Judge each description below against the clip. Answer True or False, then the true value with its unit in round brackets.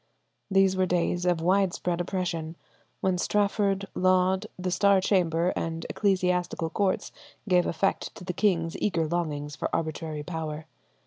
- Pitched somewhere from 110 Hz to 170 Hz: False (180 Hz)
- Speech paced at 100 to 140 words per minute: True (135 wpm)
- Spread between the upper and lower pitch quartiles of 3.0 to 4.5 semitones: False (2.4 semitones)